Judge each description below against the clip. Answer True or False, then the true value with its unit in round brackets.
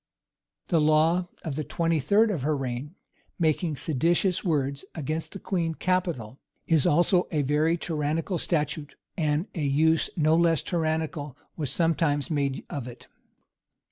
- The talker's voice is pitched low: False (155 Hz)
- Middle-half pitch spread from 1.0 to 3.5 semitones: True (2.5 semitones)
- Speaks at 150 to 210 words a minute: False (140 wpm)